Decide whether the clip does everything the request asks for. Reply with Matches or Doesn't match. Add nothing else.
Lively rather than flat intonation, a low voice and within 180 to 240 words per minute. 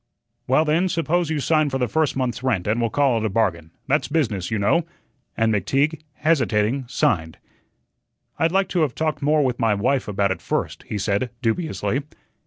Matches